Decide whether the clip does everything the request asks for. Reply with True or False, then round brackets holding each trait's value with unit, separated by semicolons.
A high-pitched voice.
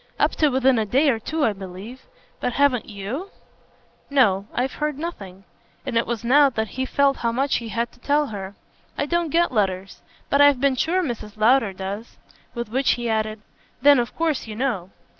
True (245 Hz)